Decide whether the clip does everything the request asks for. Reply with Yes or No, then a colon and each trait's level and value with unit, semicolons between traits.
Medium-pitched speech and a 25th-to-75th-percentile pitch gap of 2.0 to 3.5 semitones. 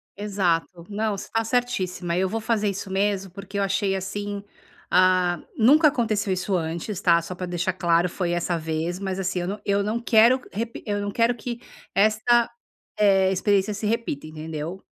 No: high, 195 Hz; average, 3.1 semitones